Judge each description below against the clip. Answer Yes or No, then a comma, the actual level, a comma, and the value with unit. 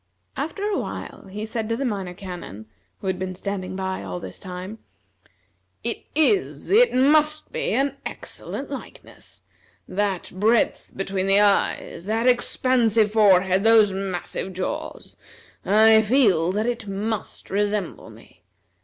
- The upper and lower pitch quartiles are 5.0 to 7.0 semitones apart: No, average, 3.5 semitones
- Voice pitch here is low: No, high, 205 Hz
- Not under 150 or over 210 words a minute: No, slow, 135 wpm